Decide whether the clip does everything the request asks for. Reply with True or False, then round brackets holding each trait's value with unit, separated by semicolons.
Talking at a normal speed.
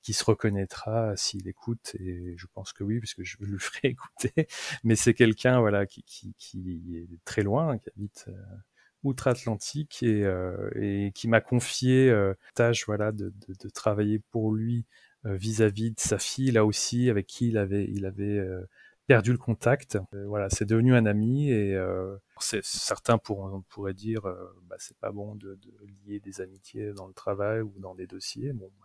True (195 wpm)